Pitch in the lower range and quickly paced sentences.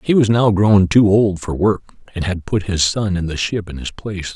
Yes: very low, 95 Hz; fast, 260 wpm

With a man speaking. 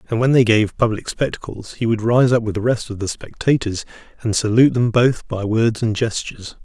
Yes: male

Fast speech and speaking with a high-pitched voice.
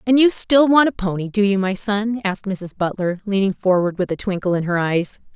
Yes: fast, 235 wpm; high, 200 Hz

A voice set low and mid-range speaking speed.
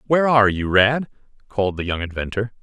Yes: low, 110 Hz; average, 185 wpm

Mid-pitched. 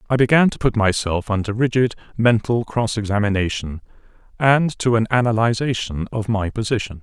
No: low, 110 Hz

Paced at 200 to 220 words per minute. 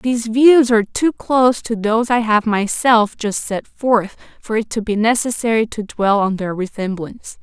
No: average, 185 wpm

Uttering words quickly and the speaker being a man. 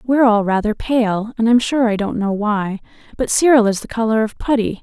No: fast, 225 wpm; female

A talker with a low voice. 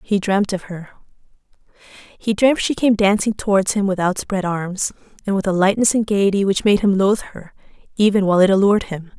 No: high, 195 Hz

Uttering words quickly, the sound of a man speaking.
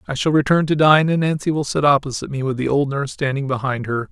Yes: fast, 265 wpm; male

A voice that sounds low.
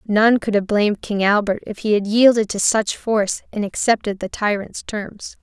No: high, 210 Hz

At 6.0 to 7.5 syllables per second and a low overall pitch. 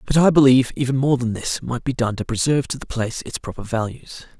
Yes: 6.3 syllables/s; low, 130 Hz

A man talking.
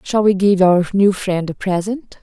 No: female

